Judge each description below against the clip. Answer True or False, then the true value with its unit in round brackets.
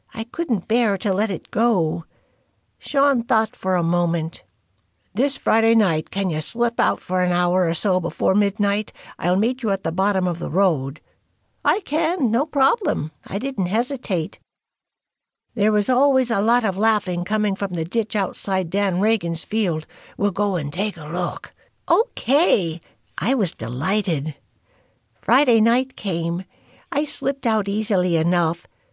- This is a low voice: False (200 Hz)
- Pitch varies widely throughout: False (4.7 semitones)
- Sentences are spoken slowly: False (155 wpm)